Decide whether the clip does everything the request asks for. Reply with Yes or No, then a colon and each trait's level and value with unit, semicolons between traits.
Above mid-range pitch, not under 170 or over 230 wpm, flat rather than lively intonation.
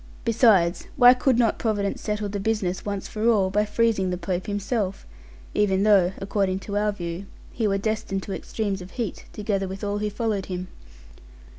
Yes: high, 205 Hz; average, 180 wpm; narrow, 2.1 semitones